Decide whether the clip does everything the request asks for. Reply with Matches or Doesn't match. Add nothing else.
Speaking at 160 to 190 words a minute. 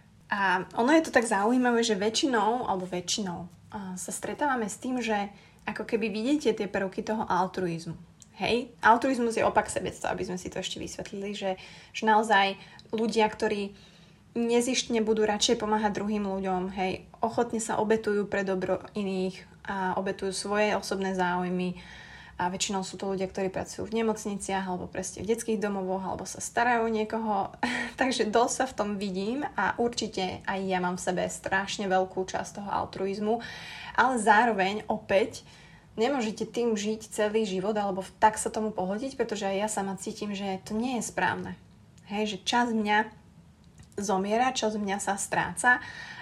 Matches